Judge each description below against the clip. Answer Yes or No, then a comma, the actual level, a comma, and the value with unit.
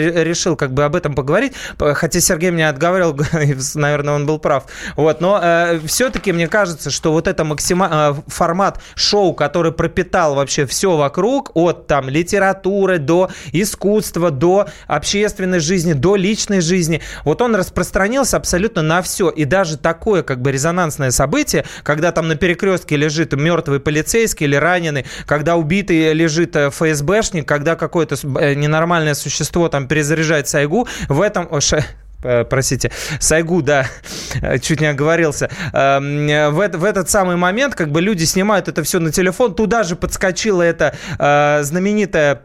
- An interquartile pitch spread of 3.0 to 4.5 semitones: Yes, average, 3.9 semitones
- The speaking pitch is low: No, medium, 165 Hz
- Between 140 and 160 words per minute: Yes, average, 150 wpm